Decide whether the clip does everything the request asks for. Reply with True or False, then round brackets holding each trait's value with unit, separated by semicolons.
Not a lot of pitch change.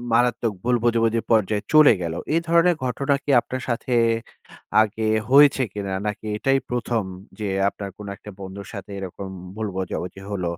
False (3.7 semitones)